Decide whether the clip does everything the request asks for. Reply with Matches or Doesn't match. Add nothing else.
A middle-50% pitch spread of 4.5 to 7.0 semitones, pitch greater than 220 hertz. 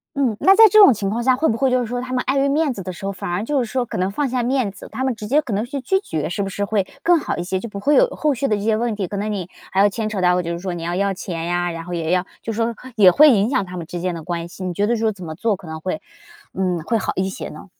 Doesn't match